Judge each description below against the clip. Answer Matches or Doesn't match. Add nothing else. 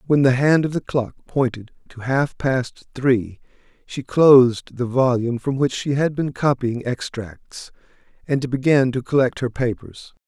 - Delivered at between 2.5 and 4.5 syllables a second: Matches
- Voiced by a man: Matches